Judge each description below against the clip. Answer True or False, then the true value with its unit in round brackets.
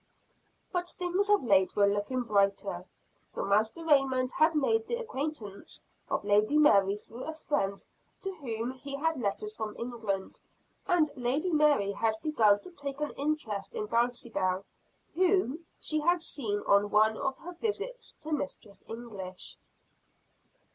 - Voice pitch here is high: True (255 Hz)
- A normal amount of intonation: False (7.0 semitones)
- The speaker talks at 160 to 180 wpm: False (145 wpm)